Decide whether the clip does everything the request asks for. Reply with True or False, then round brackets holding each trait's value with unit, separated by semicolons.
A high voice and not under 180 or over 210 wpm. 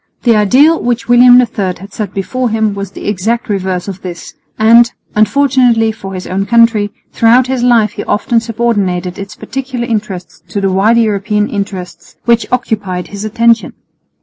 False (215 Hz; 165 wpm)